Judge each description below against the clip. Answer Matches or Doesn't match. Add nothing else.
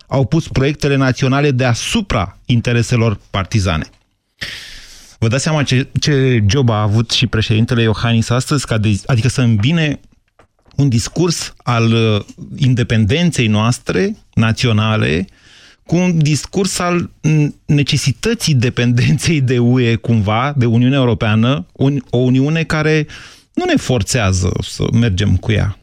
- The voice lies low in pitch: Matches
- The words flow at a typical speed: Matches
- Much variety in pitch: Doesn't match